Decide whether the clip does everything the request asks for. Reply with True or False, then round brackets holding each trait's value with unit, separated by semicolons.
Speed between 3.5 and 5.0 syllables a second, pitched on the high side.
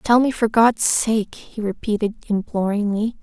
True (4.4 syllables/s; 215 Hz)